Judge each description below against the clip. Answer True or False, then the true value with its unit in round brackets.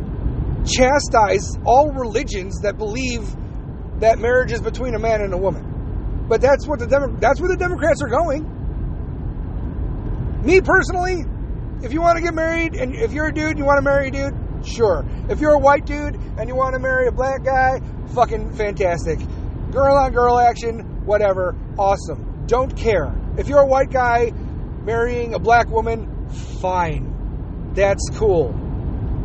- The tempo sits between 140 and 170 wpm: True (165 wpm)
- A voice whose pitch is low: False (260 Hz)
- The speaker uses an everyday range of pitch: True (4.2 semitones)